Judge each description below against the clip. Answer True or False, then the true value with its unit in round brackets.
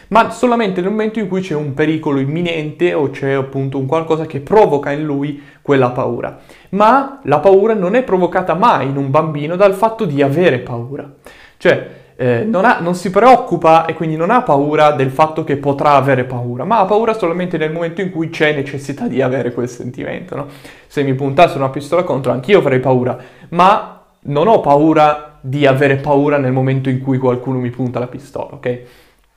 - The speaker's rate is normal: False (195 wpm)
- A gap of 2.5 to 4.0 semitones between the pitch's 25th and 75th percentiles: False (4.6 semitones)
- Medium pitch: True (150 Hz)